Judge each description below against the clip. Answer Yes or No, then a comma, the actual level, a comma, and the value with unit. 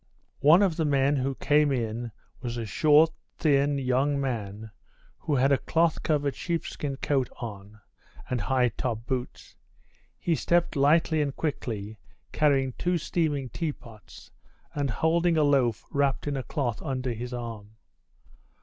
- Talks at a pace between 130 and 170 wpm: Yes, average, 145 wpm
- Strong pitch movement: No, average, 3.8 semitones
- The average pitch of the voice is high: No, low, 135 Hz